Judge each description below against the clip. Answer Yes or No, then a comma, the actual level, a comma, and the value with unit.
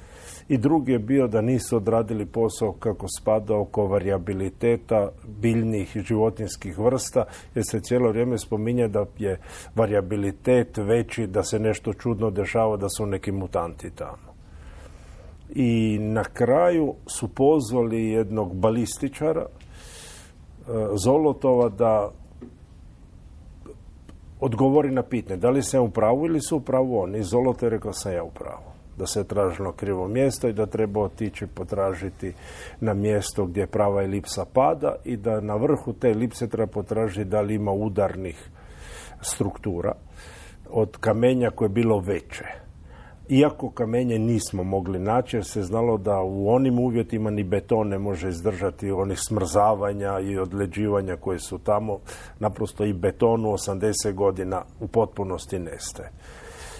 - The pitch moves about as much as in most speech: Yes, average, 3.1 semitones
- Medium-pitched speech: No, low, 105 Hz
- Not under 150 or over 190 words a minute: No, average, 135 wpm